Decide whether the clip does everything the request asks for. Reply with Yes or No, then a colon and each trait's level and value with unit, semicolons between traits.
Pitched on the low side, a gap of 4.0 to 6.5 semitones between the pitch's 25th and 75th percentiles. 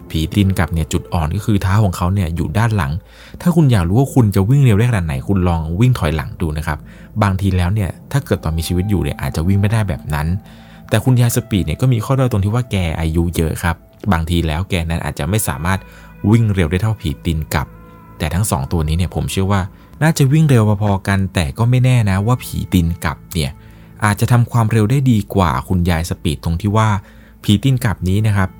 Yes: low, 100 Hz; average, 4.7 semitones